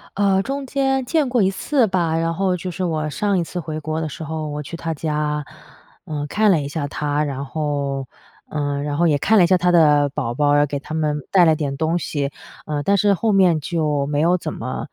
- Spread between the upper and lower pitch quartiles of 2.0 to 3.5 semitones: No, average, 4.0 semitones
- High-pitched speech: No, medium, 160 Hz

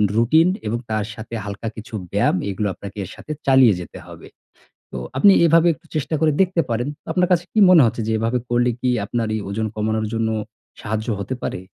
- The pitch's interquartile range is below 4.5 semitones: No, average, 5.3 semitones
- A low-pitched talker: Yes, low, 115 Hz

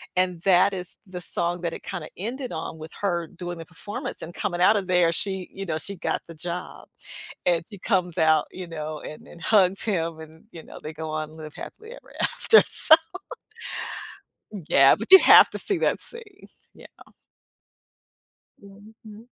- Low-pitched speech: No, medium, 180 Hz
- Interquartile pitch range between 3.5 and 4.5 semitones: Yes, average, 3.8 semitones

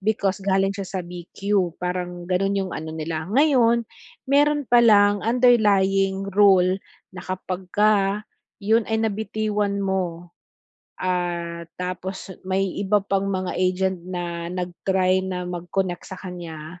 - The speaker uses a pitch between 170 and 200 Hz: Yes, high, 190 Hz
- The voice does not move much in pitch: Yes, narrow, 2.2 semitones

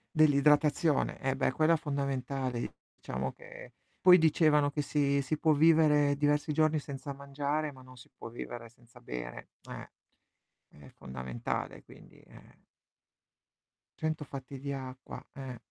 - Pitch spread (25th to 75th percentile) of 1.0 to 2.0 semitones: No, average, 2.8 semitones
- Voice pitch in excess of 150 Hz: No, medium, 140 Hz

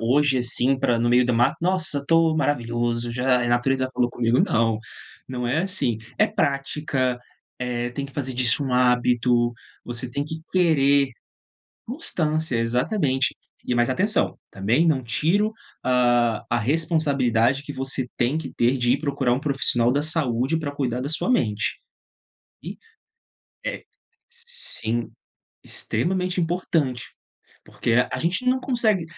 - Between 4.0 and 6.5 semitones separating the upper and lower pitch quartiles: Yes, average, 4.5 semitones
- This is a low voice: Yes, low, 130 Hz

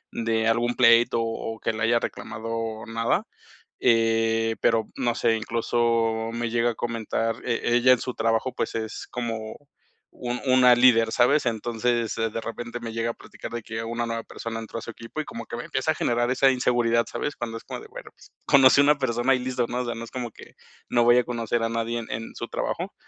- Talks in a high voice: No, low, 115 Hz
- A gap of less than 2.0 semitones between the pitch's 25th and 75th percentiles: Yes, narrow, 1.2 semitones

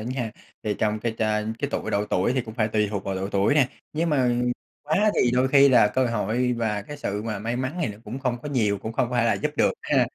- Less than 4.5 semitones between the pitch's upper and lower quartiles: Yes, average, 3.6 semitones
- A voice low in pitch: Yes, low, 115 Hz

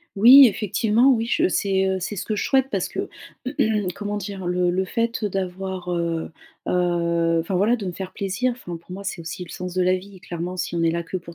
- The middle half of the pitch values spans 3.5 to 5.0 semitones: No, average, 2.9 semitones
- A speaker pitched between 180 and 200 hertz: Yes, medium, 185 Hz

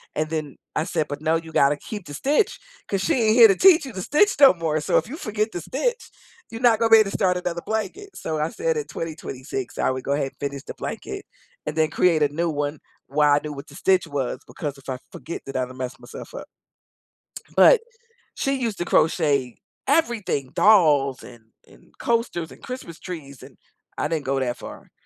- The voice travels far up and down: Yes, wide, 7.5 semitones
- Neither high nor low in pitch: Yes, medium, 165 Hz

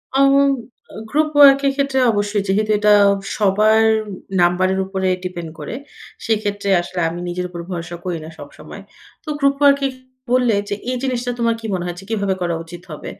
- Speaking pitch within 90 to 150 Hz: No, high, 205 Hz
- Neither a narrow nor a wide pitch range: No, wide, 5.7 semitones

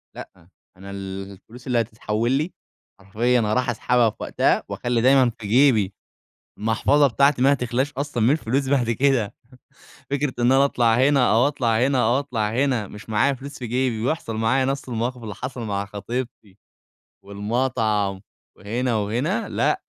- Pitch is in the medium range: No, low, 120 Hz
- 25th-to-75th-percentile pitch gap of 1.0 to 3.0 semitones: No, average, 3.6 semitones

